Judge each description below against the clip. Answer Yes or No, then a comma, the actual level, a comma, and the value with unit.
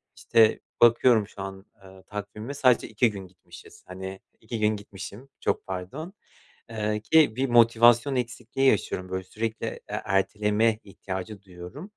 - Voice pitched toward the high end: No, low, 105 Hz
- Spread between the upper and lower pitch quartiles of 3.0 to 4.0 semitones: Yes, average, 3.5 semitones